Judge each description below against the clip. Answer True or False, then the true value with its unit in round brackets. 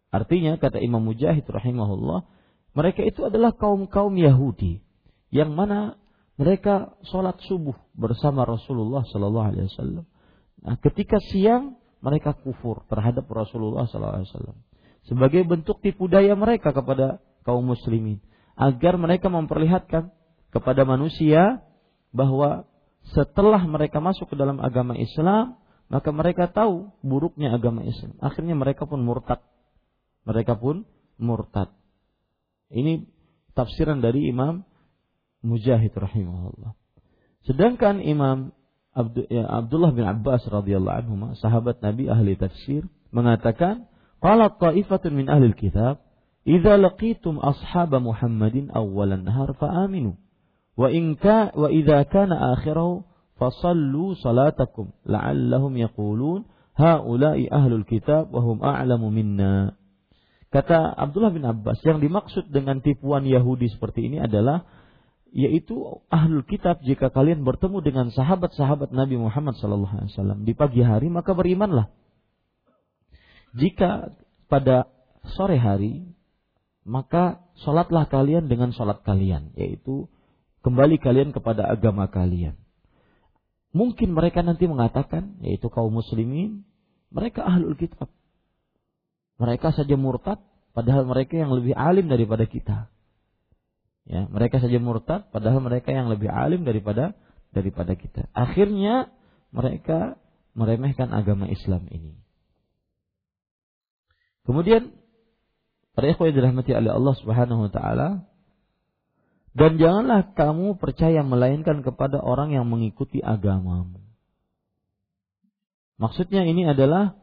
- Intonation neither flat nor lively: False (7.0 semitones)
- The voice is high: False (135 Hz)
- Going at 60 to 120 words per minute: True (110 wpm)